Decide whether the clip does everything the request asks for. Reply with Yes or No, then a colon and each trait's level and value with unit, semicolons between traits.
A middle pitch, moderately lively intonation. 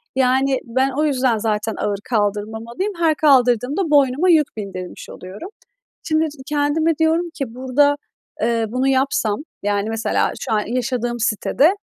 No: very high, 255 Hz; average, 4.7 semitones